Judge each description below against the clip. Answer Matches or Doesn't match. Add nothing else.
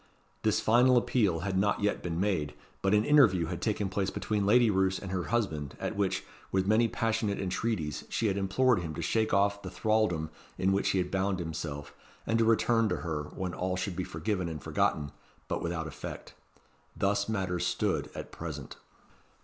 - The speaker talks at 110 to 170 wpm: Doesn't match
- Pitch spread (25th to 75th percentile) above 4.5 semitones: Doesn't match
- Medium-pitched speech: Doesn't match